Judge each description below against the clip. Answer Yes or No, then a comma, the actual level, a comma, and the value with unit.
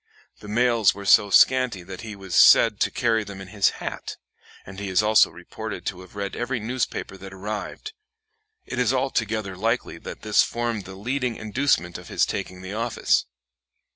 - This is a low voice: Yes, low, 105 Hz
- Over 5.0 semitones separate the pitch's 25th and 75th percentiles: No, average, 3.5 semitones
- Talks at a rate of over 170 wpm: Yes, average, 180 wpm